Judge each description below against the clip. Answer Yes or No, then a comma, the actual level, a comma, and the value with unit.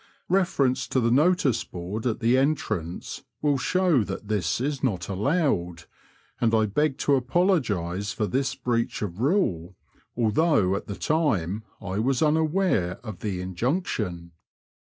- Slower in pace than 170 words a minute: Yes, average, 140 wpm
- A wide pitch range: Yes, wide, 7.2 semitones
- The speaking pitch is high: No, low, 115 Hz